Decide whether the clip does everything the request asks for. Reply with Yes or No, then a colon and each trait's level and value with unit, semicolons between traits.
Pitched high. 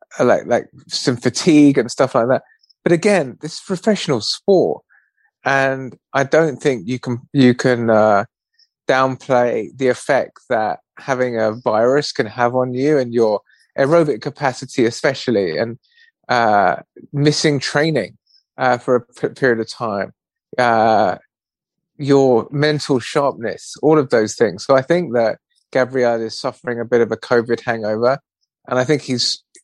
No: low, 135 Hz